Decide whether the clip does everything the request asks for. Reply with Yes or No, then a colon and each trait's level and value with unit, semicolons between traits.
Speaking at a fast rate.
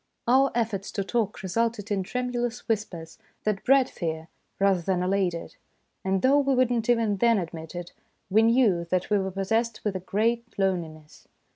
No: average, 185 wpm